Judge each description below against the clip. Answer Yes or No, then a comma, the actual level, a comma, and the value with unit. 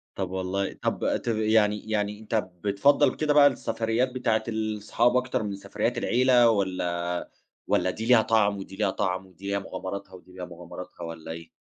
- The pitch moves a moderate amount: Yes, average, 3.5 semitones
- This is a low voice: Yes, low, 105 Hz